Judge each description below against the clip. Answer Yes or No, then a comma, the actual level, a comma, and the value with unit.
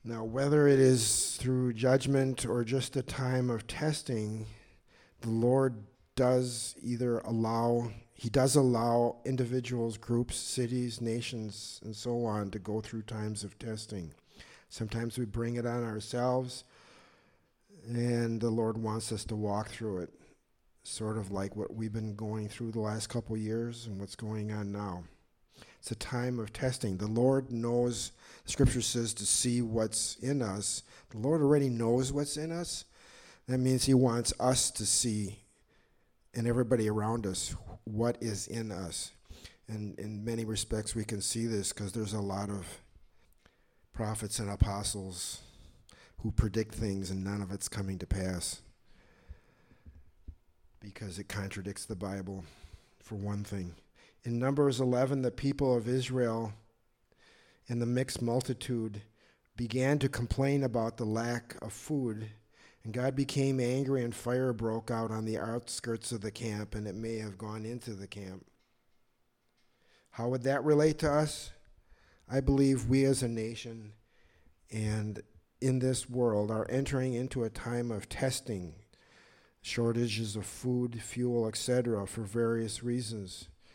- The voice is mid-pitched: No, low, 115 Hz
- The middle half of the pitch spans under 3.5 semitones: Yes, average, 2.9 semitones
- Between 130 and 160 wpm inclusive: Yes, average, 150 wpm